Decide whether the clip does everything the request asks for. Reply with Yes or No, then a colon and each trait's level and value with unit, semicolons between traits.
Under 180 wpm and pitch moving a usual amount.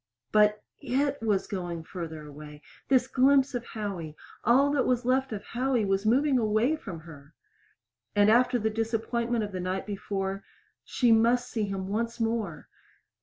Yes: average, 160 wpm; average, 4.3 semitones